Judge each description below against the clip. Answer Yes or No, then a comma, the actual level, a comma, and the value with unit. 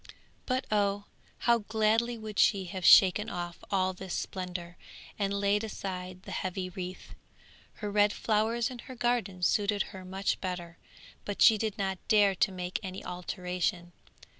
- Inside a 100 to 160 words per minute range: Yes, average, 155 wpm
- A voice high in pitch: Yes, high, 195 Hz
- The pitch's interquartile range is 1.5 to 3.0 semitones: Yes, average, 2.7 semitones